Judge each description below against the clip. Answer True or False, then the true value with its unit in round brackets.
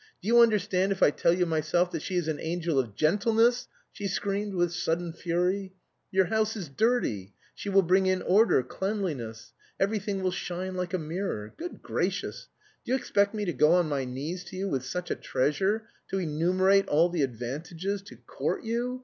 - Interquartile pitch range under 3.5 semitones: False (3.9 semitones)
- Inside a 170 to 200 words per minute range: True (190 wpm)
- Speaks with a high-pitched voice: False (180 Hz)